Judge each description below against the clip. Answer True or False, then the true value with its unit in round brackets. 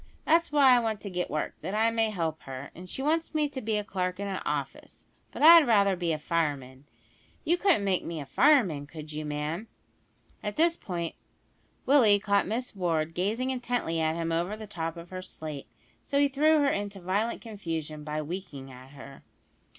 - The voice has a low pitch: False (190 Hz)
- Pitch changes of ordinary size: False (6.5 semitones)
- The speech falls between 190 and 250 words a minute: True (200 wpm)